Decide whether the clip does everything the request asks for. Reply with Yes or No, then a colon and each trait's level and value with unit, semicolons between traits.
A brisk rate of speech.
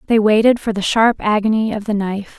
Yes: fast, 225 wpm